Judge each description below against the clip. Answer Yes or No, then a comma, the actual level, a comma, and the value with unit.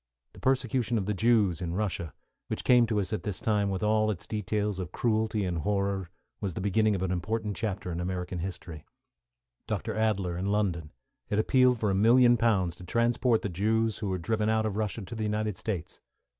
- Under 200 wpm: No, fast, 205 wpm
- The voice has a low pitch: Yes, low, 105 Hz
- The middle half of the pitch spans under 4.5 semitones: Yes, average, 3.0 semitones